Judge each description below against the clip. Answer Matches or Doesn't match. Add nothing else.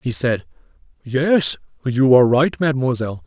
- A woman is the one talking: Doesn't match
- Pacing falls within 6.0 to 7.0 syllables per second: Doesn't match